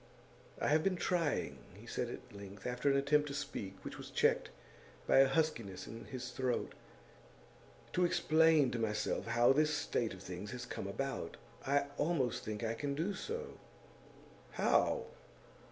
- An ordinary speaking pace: Yes, average, 160 wpm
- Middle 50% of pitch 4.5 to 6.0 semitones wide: Yes, average, 5.3 semitones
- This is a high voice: No, low, 135 Hz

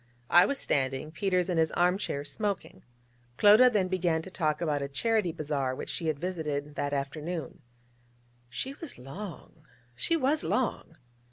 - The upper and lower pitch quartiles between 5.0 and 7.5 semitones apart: Yes, wide, 5.5 semitones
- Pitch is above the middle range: No, medium, 165 Hz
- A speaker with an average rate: Yes, average, 160 wpm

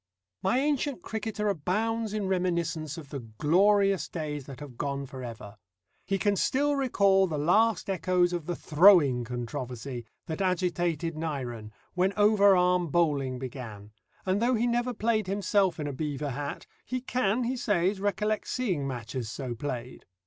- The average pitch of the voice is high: No, medium, 175 Hz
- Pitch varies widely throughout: Yes, wide, 6.7 semitones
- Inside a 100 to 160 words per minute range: Yes, average, 155 wpm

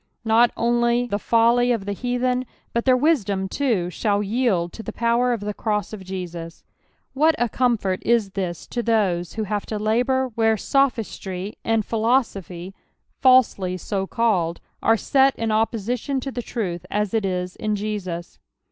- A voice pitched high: Yes, high, 220 Hz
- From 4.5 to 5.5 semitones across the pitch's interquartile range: No, average, 3.8 semitones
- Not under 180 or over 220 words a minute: No, average, 165 wpm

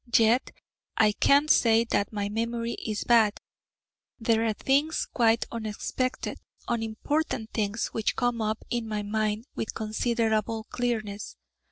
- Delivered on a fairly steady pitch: Yes, narrow, 1.7 semitones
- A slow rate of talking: Yes, slow, 130 wpm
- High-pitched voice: Yes, high, 225 Hz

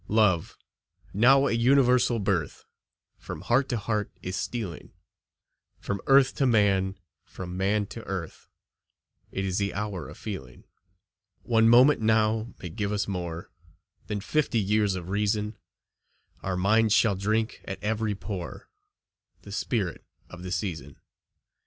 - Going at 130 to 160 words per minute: Yes, slow, 135 wpm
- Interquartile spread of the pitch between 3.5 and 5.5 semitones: No, average, 3.0 semitones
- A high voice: No, low, 105 Hz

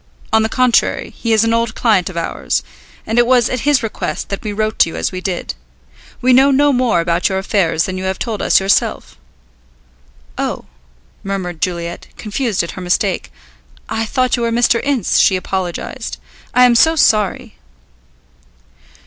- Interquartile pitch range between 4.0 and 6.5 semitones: Yes, average, 4.5 semitones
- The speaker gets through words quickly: No, average, 175 wpm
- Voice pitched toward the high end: Yes, high, 215 Hz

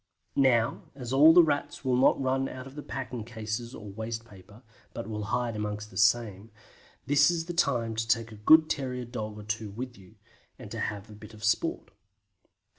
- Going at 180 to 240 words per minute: Yes, average, 200 wpm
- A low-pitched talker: Yes, low, 115 Hz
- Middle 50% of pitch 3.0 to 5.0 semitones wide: Yes, average, 3.7 semitones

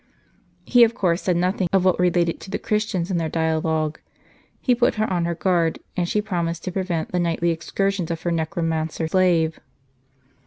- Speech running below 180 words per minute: No, average, 185 wpm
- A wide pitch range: No, narrow, 2.4 semitones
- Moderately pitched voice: Yes, medium, 175 Hz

